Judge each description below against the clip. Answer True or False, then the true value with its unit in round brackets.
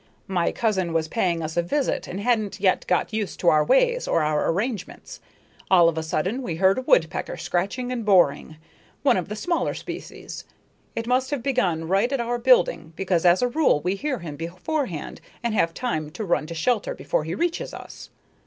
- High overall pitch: True (195 Hz)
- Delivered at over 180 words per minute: True (200 wpm)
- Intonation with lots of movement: True (6.9 semitones)